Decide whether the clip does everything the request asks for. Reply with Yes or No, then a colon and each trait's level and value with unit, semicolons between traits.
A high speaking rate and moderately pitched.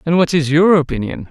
Yes: fast, 230 wpm; medium, 160 Hz